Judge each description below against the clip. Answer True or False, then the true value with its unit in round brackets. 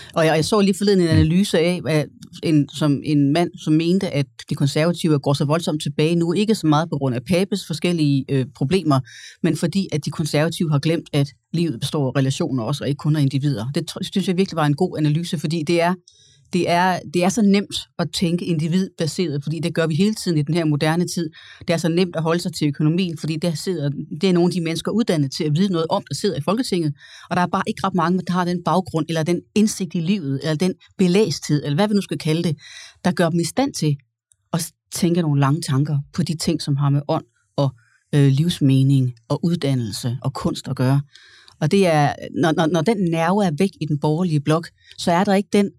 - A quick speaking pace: True (235 wpm)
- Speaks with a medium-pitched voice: True (165 Hz)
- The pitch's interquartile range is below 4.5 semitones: True (3.6 semitones)